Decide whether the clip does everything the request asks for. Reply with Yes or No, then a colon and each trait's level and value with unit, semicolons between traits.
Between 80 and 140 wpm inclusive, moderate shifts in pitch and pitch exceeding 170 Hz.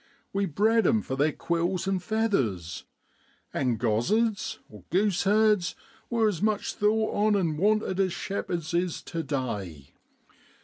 No: slow, 135 wpm; wide, 6.3 semitones; medium, 185 Hz